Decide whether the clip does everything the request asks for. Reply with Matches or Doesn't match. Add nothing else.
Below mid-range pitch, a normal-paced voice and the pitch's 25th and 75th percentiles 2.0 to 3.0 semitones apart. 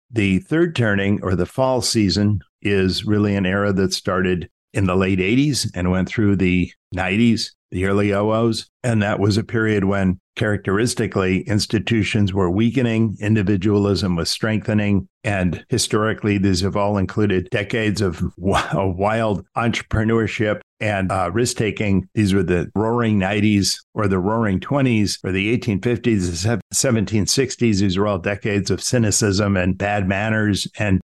Matches